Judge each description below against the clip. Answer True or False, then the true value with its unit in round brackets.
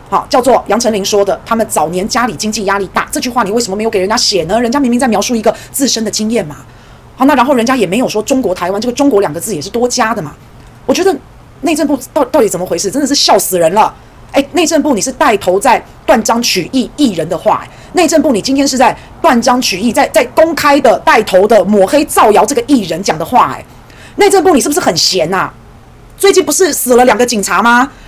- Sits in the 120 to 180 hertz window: False (240 Hz)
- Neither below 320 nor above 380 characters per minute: True (355 characters per minute)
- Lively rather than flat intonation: True (5.7 semitones)